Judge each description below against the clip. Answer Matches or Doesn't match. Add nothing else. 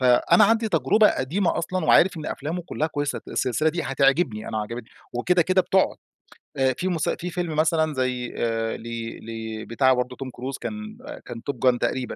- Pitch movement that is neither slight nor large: Doesn't match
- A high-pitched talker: Doesn't match